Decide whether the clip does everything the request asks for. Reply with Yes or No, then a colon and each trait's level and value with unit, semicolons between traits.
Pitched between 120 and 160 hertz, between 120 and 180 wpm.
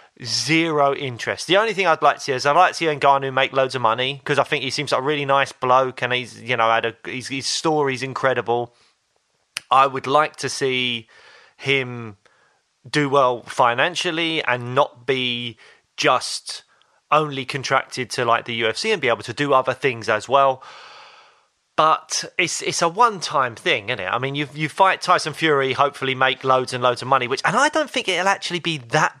No: low, 135 Hz; fast, 205 wpm